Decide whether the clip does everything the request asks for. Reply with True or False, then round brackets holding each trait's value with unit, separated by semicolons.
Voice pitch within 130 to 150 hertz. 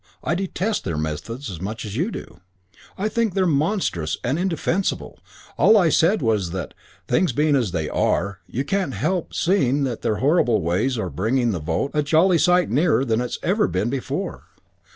True (135 Hz)